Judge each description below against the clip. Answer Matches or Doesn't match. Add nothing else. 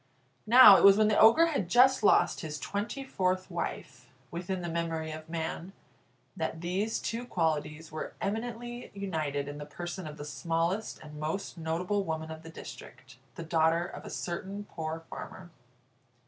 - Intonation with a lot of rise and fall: Doesn't match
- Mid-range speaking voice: Matches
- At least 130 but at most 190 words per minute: Matches